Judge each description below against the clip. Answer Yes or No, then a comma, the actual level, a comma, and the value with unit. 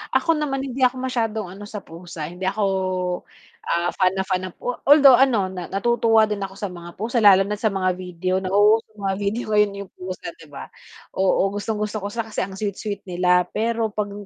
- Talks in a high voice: Yes, high, 205 Hz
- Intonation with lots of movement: No, average, 3.2 semitones